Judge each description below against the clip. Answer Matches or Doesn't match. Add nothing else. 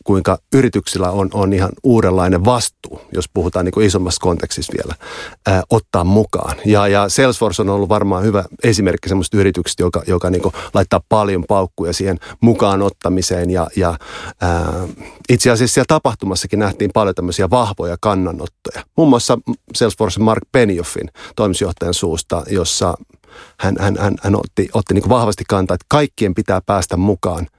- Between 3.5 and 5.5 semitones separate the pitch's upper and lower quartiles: Doesn't match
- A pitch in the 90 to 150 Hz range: Matches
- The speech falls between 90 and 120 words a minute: Doesn't match